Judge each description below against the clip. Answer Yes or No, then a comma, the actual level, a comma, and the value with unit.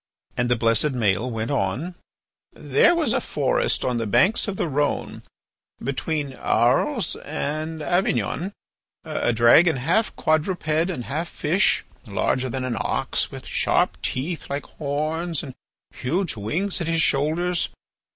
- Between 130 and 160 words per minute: Yes, average, 140 wpm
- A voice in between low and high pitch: Yes, medium, 150 Hz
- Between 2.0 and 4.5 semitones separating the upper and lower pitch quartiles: No, wide, 5.5 semitones